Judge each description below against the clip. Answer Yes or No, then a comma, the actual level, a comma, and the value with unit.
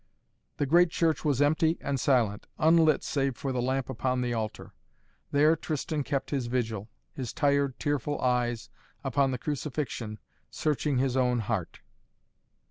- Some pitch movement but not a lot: Yes, average, 3.1 semitones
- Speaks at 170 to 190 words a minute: No, average, 145 wpm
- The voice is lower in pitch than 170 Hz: Yes, low, 135 Hz